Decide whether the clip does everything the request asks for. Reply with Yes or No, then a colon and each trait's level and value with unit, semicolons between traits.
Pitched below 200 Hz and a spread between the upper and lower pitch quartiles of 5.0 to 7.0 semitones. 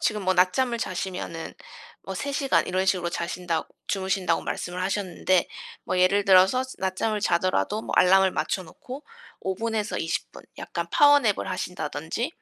No: high, 190 Hz; average, 2.8 semitones